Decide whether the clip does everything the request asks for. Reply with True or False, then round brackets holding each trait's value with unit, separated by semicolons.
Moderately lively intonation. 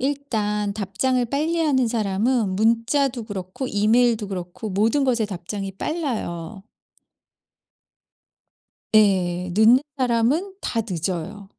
True (4.7 semitones)